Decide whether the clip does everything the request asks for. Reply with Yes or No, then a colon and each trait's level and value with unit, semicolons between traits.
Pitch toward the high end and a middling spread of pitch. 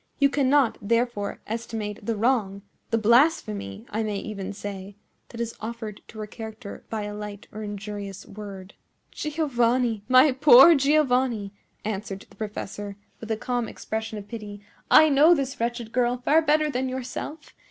Yes: high, 225 Hz; average, 3.7 semitones